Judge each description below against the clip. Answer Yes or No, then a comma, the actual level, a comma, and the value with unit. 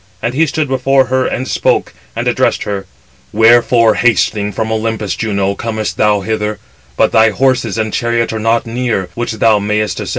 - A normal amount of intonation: No, narrow, 2.2 semitones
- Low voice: Yes, low, 110 Hz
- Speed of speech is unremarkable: Yes, average, 175 wpm